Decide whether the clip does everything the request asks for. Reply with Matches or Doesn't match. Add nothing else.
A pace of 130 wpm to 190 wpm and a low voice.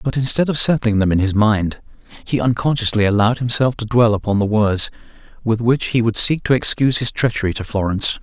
Doesn't match